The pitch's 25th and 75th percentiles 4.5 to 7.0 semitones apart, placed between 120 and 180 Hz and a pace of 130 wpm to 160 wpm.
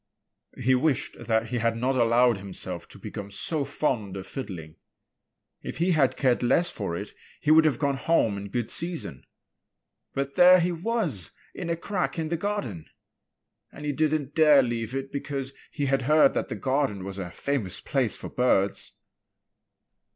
No: wide, 5.6 semitones; low, 135 Hz; average, 175 wpm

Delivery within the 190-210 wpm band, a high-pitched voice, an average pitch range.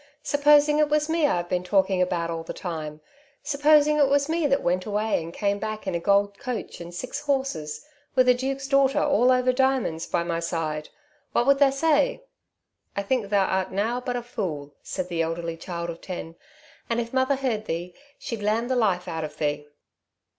No: average, 200 wpm; high, 210 Hz; wide, 7.9 semitones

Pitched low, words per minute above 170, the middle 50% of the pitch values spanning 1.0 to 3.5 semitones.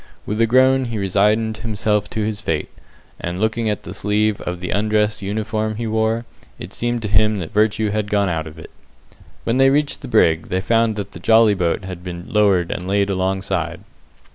Yes: low, 105 Hz; average, 200 wpm; average, 2.8 semitones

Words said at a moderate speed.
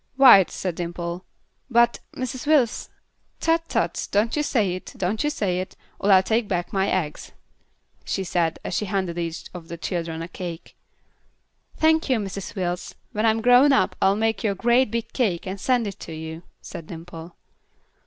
Yes: average, 185 wpm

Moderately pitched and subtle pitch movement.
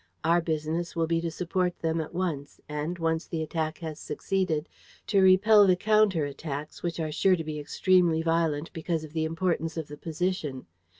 Yes: medium, 165 Hz; narrow, 2.3 semitones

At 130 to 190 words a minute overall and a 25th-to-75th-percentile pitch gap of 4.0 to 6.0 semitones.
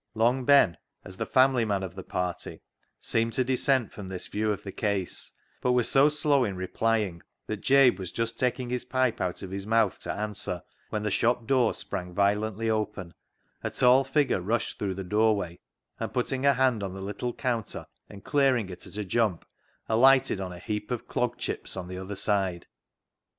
No: average, 200 wpm; average, 4.5 semitones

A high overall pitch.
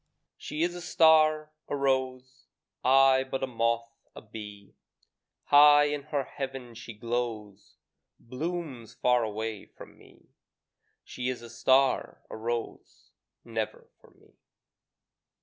No: low, 130 Hz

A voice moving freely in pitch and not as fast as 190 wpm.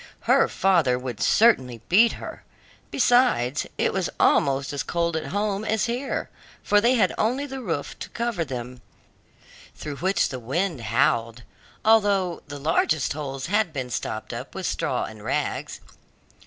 Yes: wide, 8.4 semitones; average, 155 wpm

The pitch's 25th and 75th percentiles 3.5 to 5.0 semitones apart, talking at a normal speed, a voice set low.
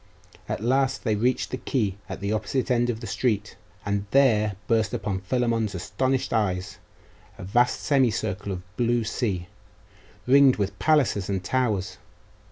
Yes: average, 3.9 semitones; average, 150 wpm; low, 110 Hz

